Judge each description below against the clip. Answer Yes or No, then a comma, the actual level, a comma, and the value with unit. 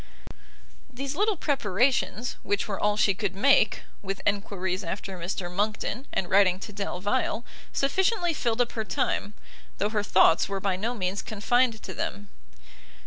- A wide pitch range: No, average, 3.9 semitones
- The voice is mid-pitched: No, high, 205 Hz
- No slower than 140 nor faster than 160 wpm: Yes, average, 150 wpm